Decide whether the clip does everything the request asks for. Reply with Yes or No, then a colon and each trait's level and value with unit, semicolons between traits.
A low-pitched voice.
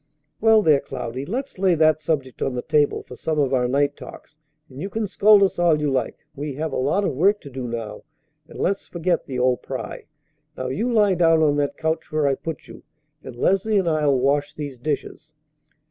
No: medium, 150 Hz